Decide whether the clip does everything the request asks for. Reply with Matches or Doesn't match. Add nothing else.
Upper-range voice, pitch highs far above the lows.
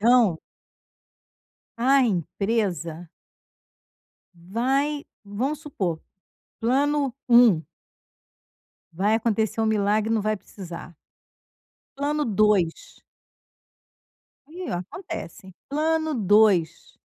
Matches